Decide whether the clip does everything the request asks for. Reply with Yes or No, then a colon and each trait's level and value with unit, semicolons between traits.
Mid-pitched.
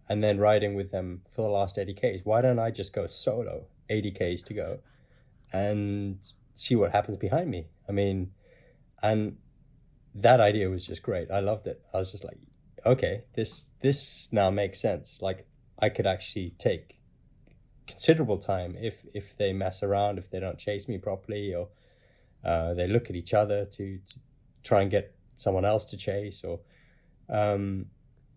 No: low, 105 Hz